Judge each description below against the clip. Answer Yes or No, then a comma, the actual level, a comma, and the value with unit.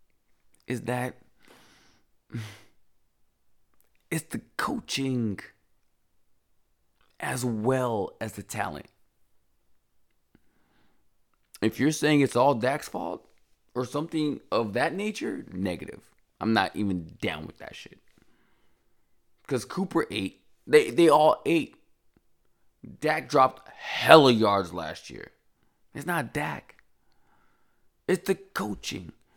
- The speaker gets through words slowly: Yes, slow, 100 wpm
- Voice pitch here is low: Yes, low, 125 Hz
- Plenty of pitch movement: Yes, wide, 6.7 semitones